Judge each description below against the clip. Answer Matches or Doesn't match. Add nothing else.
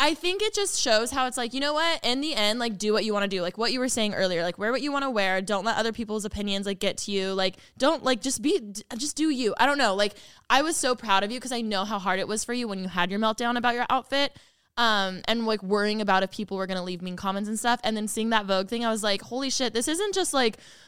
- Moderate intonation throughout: Matches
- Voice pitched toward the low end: Doesn't match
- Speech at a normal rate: Doesn't match